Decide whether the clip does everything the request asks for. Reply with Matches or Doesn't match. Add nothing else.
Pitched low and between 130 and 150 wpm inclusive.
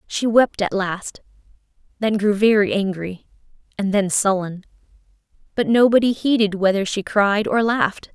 Doesn't match